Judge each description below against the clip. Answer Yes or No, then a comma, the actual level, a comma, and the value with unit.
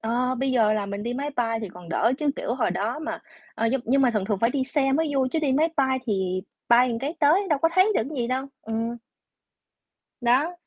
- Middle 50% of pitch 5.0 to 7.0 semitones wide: No, average, 4.1 semitones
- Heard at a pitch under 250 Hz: No, very high, 255 Hz